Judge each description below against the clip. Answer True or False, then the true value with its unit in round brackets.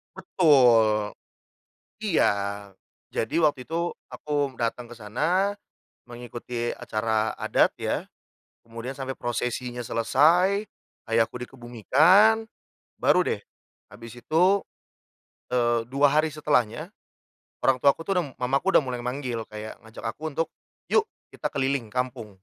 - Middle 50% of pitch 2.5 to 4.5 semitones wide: False (5.0 semitones)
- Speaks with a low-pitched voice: True (125 Hz)